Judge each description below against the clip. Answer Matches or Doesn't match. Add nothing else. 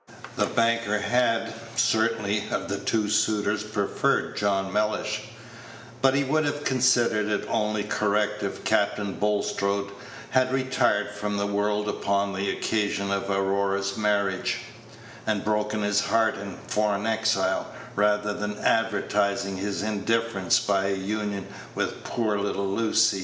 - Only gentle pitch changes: Matches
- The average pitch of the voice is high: Doesn't match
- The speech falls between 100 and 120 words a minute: Doesn't match